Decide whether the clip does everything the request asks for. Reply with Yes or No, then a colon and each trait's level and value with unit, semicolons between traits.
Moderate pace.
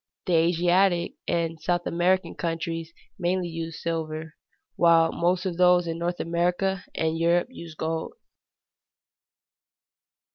No: slow, 115 wpm